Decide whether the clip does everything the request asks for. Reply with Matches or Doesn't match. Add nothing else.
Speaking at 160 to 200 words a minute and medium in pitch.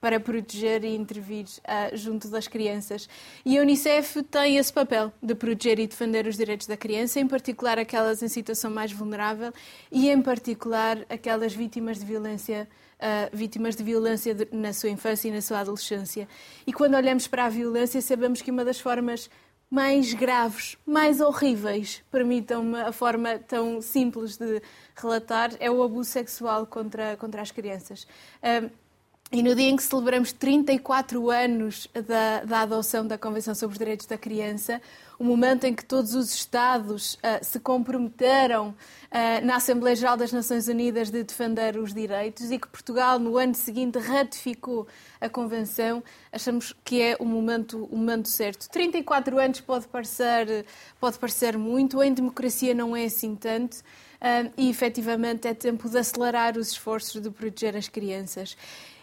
Doesn't match